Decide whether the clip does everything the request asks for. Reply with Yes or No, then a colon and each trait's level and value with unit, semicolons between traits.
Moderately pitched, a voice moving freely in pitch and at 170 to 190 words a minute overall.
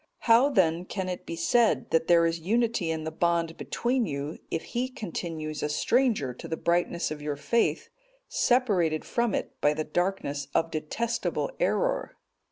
Yes: medium, 170 Hz; wide, 6.8 semitones; average, 175 wpm